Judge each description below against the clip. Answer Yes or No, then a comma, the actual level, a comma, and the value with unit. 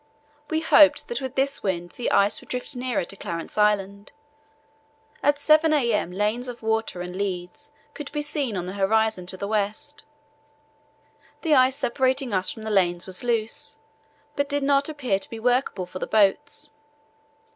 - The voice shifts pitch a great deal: Yes, wide, 6.0 semitones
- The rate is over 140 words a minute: Yes, average, 170 wpm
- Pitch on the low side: No, high, 225 Hz